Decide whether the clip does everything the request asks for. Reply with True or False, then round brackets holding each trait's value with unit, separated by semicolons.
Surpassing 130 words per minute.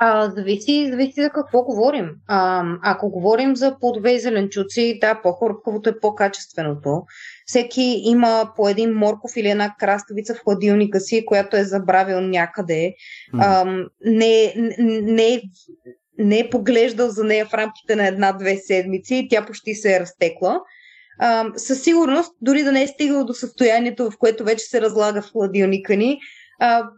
True (155 wpm)